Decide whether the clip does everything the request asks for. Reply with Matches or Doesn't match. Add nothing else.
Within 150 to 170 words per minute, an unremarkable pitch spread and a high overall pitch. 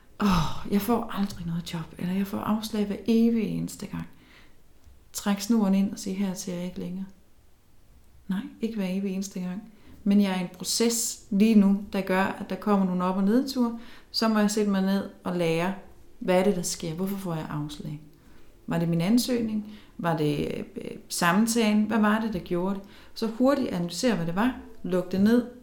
Doesn't match